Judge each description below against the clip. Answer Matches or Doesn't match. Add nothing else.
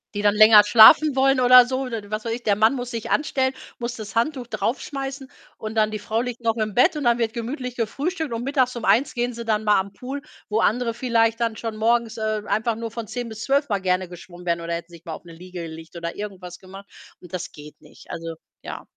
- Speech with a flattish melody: Doesn't match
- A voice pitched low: Doesn't match